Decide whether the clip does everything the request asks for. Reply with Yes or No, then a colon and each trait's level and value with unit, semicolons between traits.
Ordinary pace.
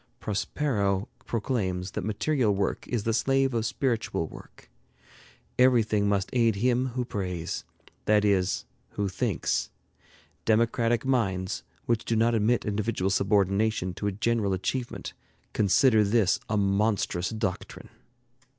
No: slow, 125 wpm